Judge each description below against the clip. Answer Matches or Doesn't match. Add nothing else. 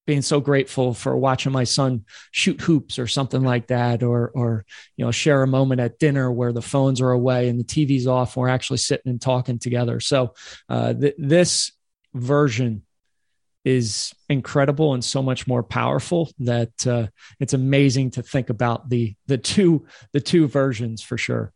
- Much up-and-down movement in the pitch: Doesn't match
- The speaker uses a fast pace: Doesn't match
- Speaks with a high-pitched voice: Doesn't match